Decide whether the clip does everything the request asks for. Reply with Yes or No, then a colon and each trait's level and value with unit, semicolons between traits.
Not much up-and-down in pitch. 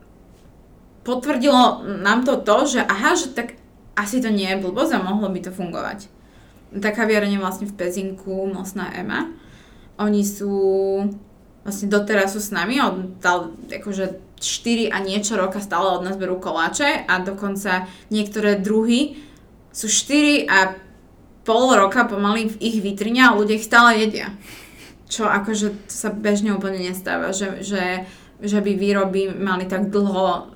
Yes: narrow, 2.3 semitones